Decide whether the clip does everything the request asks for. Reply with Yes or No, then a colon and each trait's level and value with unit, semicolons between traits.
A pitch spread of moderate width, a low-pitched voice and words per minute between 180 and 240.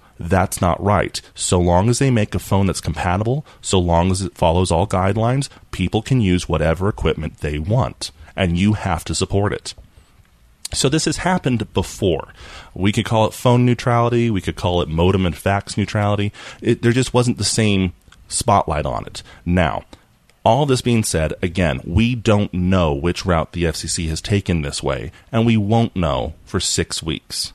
Yes: average, 4.7 semitones; very low, 95 Hz; average, 185 wpm